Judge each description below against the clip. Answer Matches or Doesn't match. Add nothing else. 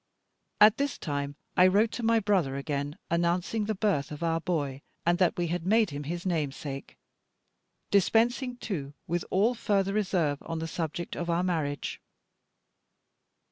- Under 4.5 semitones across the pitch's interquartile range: Doesn't match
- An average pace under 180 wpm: Matches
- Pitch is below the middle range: Doesn't match